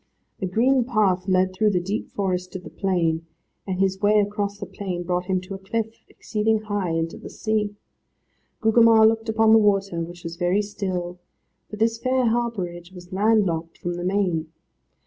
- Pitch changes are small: No, average, 3.4 semitones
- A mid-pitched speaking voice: No, high, 195 Hz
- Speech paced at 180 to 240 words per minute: Yes, average, 185 wpm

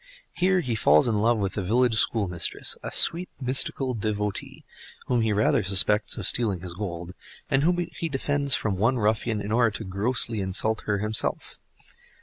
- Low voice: Yes, low, 110 Hz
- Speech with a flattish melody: No, average, 3.8 semitones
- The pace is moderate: Yes, average, 170 wpm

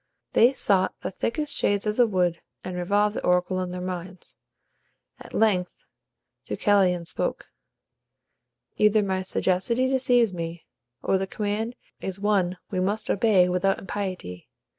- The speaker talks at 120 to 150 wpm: Yes, average, 140 wpm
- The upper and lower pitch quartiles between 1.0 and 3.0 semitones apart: Yes, average, 2.7 semitones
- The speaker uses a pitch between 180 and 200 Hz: Yes, high, 190 Hz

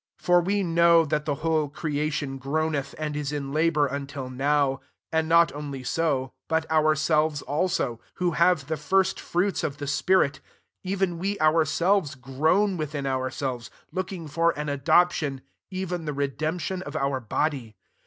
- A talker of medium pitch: Yes, medium, 155 Hz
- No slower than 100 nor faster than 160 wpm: Yes, average, 155 wpm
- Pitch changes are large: No, average, 3.2 semitones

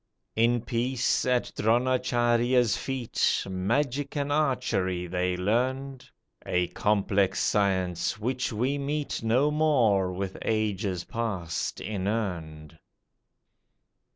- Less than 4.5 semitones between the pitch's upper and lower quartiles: No, average, 5.2 semitones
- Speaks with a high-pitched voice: No, low, 115 Hz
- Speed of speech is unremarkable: No, slow, 95 wpm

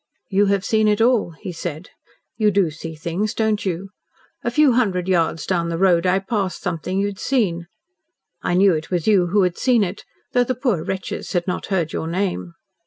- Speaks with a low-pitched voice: No, high, 190 Hz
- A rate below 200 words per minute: No, fast, 205 wpm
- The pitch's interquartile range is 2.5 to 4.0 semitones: Yes, average, 3.5 semitones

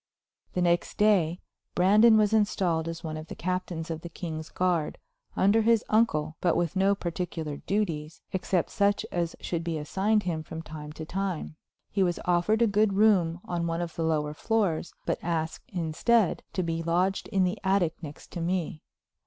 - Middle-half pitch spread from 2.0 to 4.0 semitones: Yes, average, 3.4 semitones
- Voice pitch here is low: No, medium, 175 Hz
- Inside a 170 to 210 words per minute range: Yes, average, 180 wpm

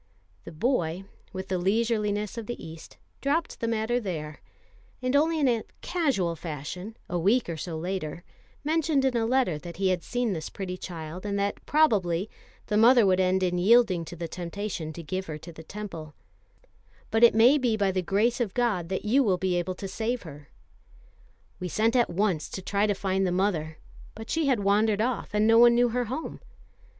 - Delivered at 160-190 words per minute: No, average, 200 wpm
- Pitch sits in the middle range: No, high, 200 Hz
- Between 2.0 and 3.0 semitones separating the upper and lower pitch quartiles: No, average, 5.0 semitones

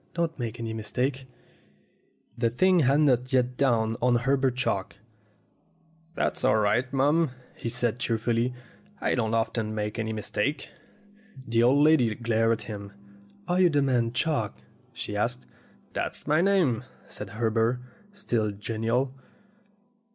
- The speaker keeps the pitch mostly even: No, average, 3.3 semitones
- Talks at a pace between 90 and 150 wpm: Yes, average, 140 wpm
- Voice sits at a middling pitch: No, low, 120 Hz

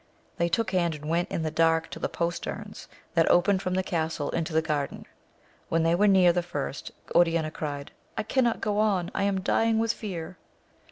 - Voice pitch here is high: No, medium, 170 Hz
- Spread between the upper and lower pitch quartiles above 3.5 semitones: No, average, 3.1 semitones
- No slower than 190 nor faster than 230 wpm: Yes, average, 200 wpm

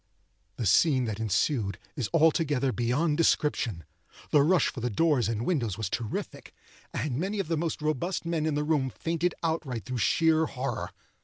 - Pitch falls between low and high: Yes, medium, 145 Hz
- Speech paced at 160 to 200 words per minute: Yes, average, 170 wpm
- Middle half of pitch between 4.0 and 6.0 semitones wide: Yes, average, 5.3 semitones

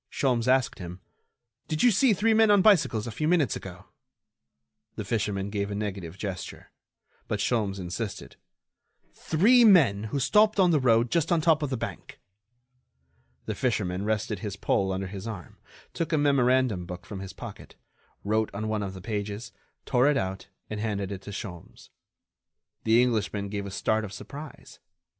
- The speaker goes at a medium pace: Yes, average, 170 wpm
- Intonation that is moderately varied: No, wide, 6.1 semitones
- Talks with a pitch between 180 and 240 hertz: No, low, 110 Hz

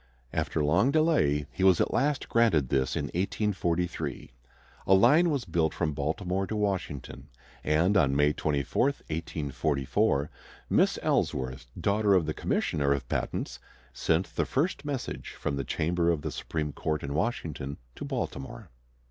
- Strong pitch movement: Yes, wide, 5.7 semitones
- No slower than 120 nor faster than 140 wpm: No, average, 150 wpm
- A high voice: No, very low, 80 Hz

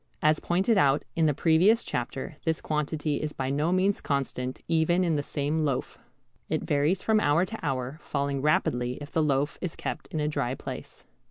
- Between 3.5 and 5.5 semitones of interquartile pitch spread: No, average, 2.9 semitones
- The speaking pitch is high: No, medium, 150 Hz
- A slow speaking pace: No, average, 190 wpm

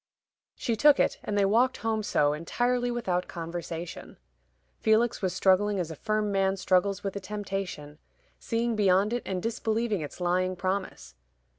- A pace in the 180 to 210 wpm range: No, average, 155 wpm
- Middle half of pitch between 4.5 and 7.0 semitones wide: No, average, 3.4 semitones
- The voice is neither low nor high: No, high, 195 Hz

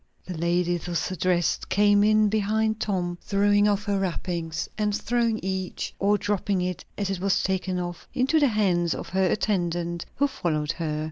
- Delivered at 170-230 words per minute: Yes, average, 175 wpm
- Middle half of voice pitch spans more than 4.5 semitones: No, average, 3.0 semitones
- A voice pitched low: No, high, 190 Hz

